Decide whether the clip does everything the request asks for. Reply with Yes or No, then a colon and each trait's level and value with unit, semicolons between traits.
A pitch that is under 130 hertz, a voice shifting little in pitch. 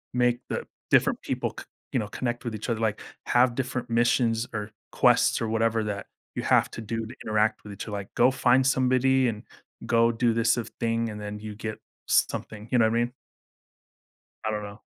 Yes: low, 115 Hz; narrow, 2.1 semitones